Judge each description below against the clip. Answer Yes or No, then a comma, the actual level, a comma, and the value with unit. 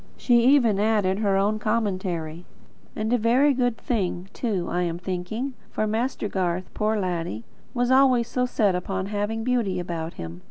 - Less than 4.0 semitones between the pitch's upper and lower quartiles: No, average, 4.5 semitones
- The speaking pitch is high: Yes, high, 205 Hz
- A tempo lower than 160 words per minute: No, average, 165 wpm